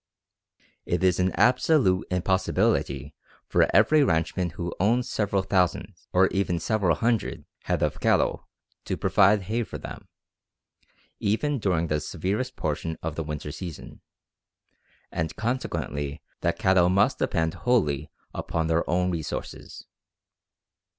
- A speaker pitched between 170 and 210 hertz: No, very low, 90 Hz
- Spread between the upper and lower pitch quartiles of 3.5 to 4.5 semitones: Yes, average, 4.2 semitones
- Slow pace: Yes, slow, 125 wpm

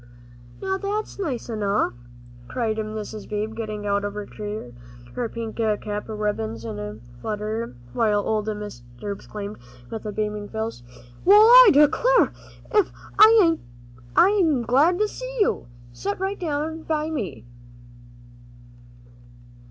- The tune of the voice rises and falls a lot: Yes, wide, 7.7 semitones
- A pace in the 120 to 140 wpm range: Yes, slow, 135 wpm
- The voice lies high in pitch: Yes, high, 220 Hz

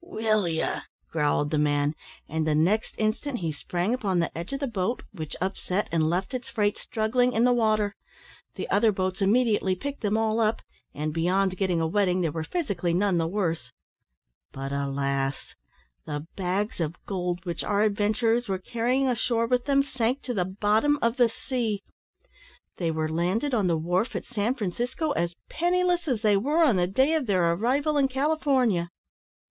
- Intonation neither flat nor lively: No, wide, 6.1 semitones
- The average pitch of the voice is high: Yes, high, 205 Hz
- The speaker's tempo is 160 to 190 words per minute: Yes, average, 180 wpm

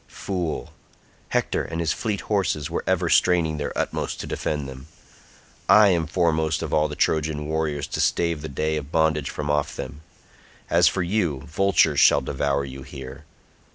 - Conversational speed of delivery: Yes, average, 170 wpm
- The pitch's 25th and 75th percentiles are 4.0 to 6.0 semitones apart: No, narrow, 2.6 semitones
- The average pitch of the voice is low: Yes, very low, 80 Hz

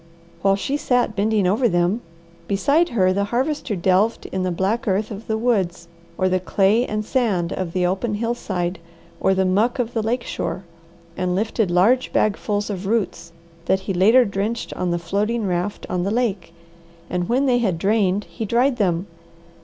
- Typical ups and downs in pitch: Yes, average, 3.9 semitones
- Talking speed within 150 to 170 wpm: No, average, 180 wpm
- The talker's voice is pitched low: No, high, 200 Hz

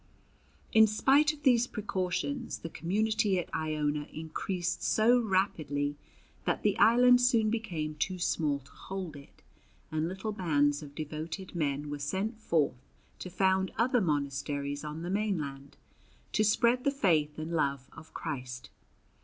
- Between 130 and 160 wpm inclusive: Yes, average, 145 wpm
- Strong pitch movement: Yes, wide, 6.4 semitones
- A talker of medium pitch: Yes, medium, 170 Hz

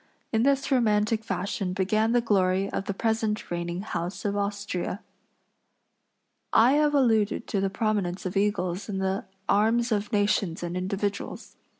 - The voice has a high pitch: Yes, high, 205 Hz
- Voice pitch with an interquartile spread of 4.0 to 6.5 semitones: No, narrow, 2.6 semitones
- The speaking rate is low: No, average, 150 wpm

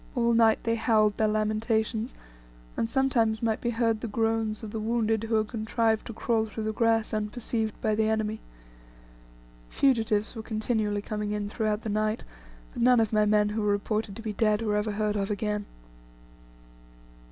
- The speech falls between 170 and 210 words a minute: Yes, average, 180 wpm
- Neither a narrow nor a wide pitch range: No, narrow, 1.2 semitones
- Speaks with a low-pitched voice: No, high, 220 Hz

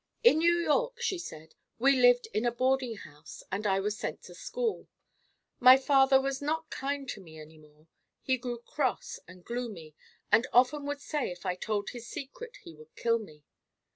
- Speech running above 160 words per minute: Yes, average, 190 wpm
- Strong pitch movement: Yes, wide, 6.6 semitones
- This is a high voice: Yes, high, 245 Hz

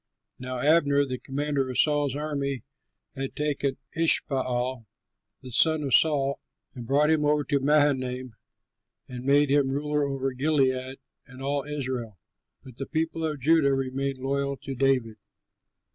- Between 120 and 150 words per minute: Yes, average, 145 wpm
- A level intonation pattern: Yes, narrow, 2.1 semitones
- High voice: No, medium, 140 Hz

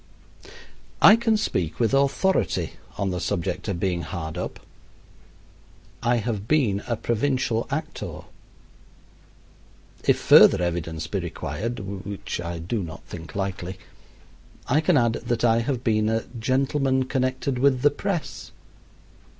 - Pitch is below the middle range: Yes, low, 115 Hz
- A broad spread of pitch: Yes, wide, 6.1 semitones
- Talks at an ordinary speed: No, slow, 130 wpm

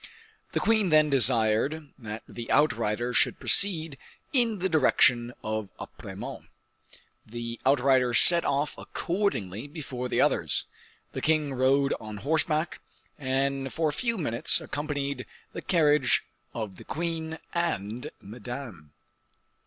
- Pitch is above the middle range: No, medium, 140 Hz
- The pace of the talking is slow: Yes, slow, 120 wpm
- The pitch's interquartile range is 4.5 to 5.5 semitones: Yes, average, 5.0 semitones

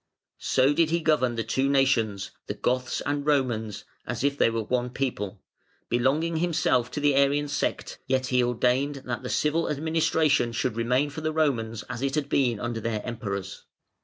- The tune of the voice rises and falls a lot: No, average, 3.7 semitones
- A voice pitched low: Yes, low, 130 Hz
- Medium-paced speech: Yes, average, 180 wpm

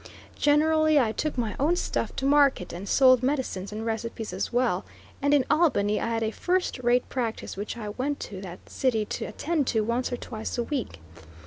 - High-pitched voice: Yes, high, 245 Hz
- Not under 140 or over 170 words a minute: No, average, 200 wpm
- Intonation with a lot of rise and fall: No, average, 4.7 semitones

